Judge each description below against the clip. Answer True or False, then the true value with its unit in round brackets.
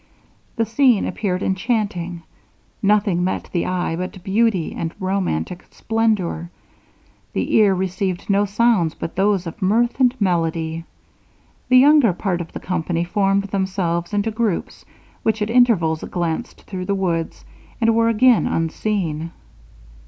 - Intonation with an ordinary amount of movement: True (4.1 semitones)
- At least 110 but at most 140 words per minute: True (135 wpm)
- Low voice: False (190 Hz)